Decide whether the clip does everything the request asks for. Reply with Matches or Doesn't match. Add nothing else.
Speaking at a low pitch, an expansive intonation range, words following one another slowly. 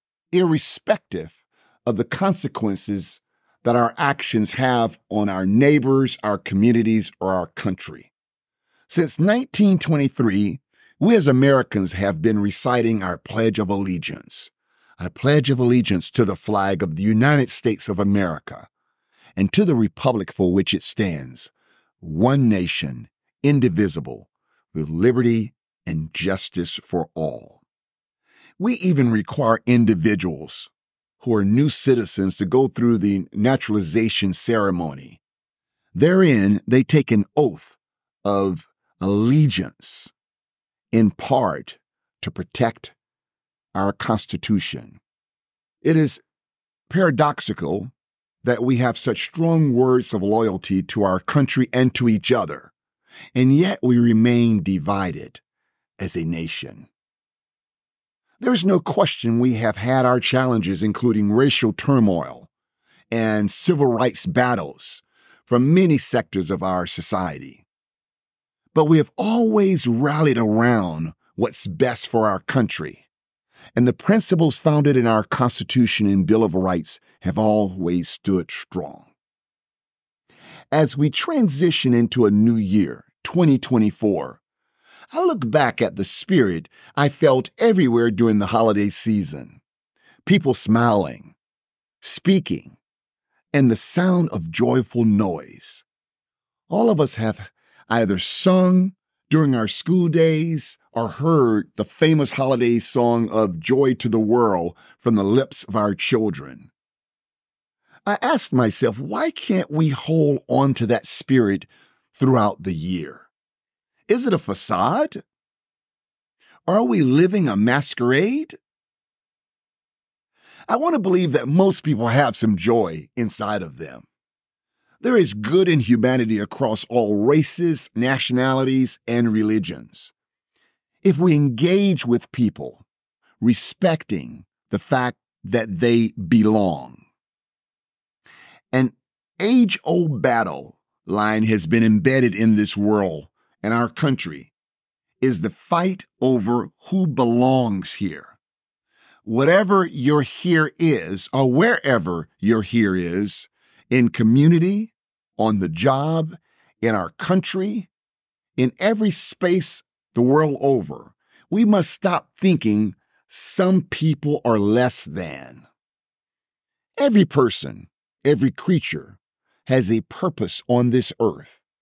Matches